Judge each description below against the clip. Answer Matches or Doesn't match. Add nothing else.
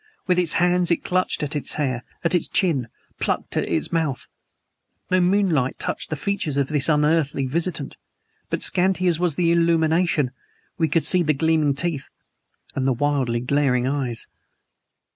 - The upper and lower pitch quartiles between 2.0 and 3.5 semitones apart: Doesn't match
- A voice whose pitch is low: Doesn't match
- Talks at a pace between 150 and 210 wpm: Matches